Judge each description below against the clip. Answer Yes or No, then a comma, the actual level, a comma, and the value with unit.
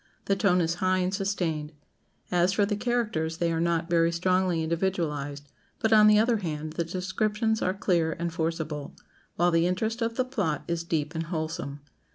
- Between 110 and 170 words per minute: No, average, 185 wpm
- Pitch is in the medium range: Yes, medium, 175 Hz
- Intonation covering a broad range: No, average, 3.5 semitones